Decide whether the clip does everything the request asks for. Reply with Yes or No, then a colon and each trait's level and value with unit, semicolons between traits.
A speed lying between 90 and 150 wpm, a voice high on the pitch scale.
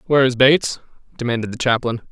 No: average, 140 wpm; low, 125 Hz